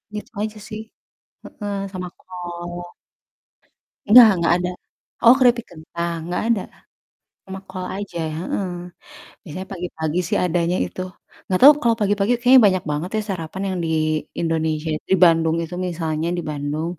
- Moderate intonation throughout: Yes, average, 3.3 semitones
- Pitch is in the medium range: Yes, medium, 180 Hz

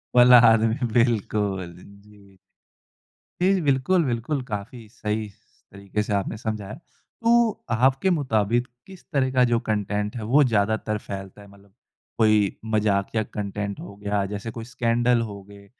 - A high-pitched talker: No, low, 110 Hz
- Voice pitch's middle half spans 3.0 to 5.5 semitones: Yes, average, 3.4 semitones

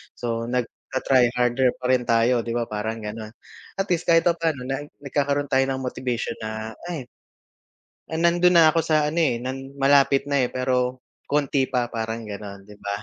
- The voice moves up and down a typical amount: Yes, average, 3.7 semitones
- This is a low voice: Yes, low, 130 Hz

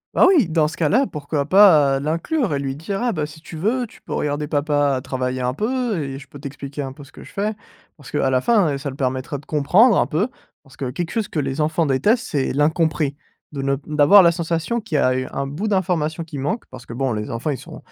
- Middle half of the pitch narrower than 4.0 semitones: No, average, 4.5 semitones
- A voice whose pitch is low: No, medium, 150 Hz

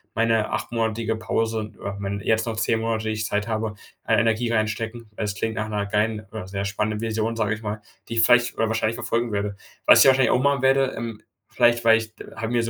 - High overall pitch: No, low, 110 Hz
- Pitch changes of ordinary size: No, narrow, 1.3 semitones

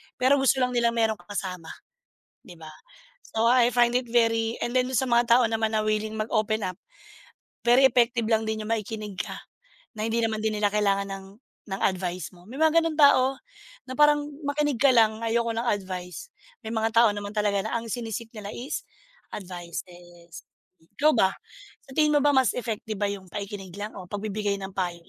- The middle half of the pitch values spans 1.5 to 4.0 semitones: Yes, average, 3.4 semitones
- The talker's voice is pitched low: No, high, 220 Hz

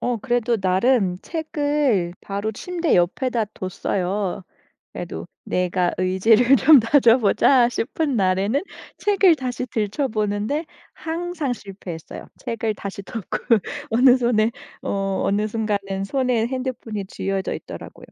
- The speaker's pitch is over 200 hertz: Yes, high, 225 Hz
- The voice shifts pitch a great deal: No, average, 5.0 semitones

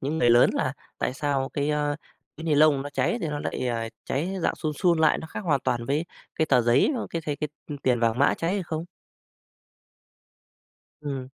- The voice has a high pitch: No, medium, 145 Hz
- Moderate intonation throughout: Yes, average, 3.3 semitones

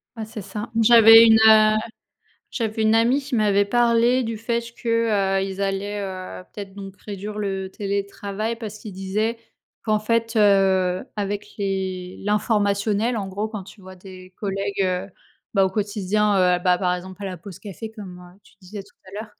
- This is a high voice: Yes, high, 205 Hz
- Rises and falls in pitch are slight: Yes, narrow, 2.2 semitones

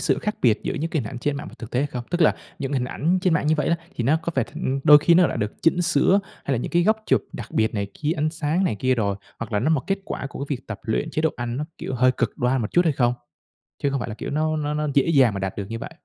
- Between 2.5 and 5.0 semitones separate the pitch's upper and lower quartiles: Yes, average, 4.7 semitones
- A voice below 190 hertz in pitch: Yes, medium, 140 Hz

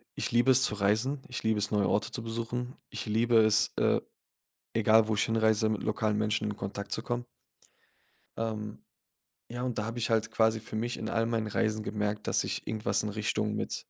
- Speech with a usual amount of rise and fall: No, narrow, 1.4 semitones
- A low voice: Yes, low, 110 Hz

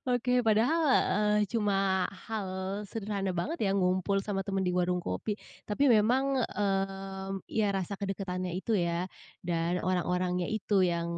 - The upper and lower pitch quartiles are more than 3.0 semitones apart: No, narrow, 2.5 semitones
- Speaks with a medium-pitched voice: No, high, 195 Hz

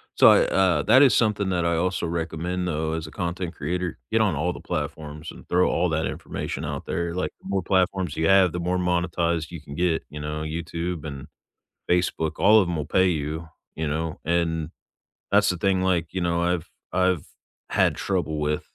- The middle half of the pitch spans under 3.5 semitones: Yes, narrow, 2.4 semitones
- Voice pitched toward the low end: Yes, very low, 85 Hz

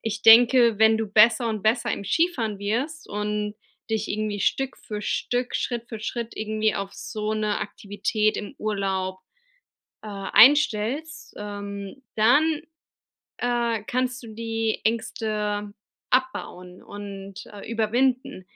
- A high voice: Yes, high, 220 Hz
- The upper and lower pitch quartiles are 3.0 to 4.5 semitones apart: No, narrow, 2.5 semitones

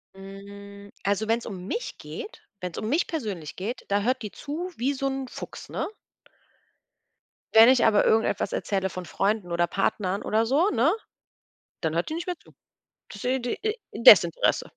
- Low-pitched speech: No, high, 220 Hz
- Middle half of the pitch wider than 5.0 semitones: Yes, wide, 5.6 semitones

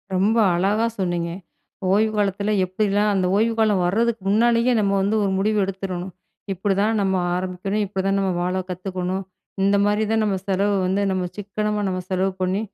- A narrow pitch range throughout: Yes, narrow, 2.1 semitones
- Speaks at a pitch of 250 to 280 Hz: No, high, 195 Hz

